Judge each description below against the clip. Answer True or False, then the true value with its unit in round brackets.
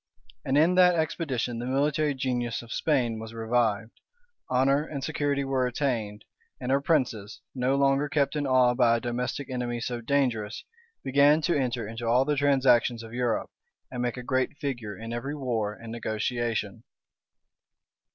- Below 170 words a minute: True (160 wpm)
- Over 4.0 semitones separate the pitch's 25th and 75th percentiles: False (3.1 semitones)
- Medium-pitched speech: False (125 Hz)